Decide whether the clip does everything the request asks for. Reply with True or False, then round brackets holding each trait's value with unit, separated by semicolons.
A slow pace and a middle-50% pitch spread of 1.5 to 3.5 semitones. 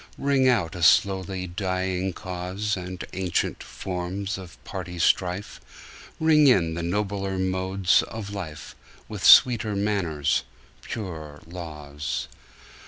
True (110 wpm; 2.4 semitones)